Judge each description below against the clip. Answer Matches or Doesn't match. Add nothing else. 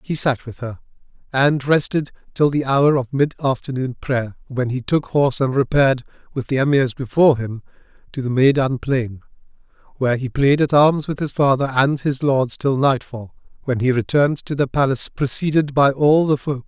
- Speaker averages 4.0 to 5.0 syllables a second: Doesn't match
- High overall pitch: Doesn't match